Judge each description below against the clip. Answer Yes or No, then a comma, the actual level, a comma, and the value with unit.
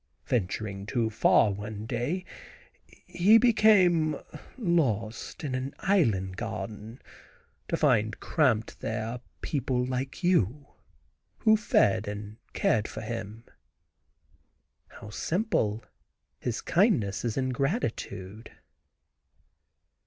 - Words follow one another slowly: Yes, slow, 100 wpm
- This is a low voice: Yes, low, 120 Hz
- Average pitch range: No, wide, 7.1 semitones